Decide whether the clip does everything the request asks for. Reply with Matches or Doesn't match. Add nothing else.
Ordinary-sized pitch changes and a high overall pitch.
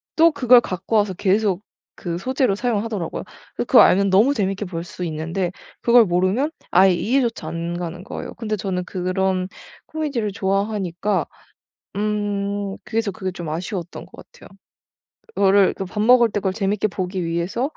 Matches